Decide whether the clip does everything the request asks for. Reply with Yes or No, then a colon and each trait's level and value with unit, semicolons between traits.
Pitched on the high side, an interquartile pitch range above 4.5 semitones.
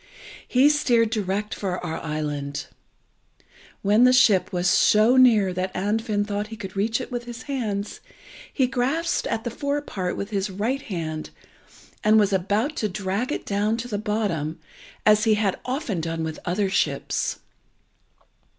No: high, 210 Hz; average, 4.1 semitones